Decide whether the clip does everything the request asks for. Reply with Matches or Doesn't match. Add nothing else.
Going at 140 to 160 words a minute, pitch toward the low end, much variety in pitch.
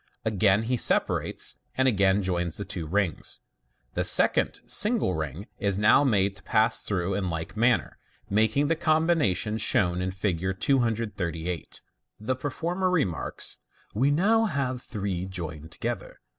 Matches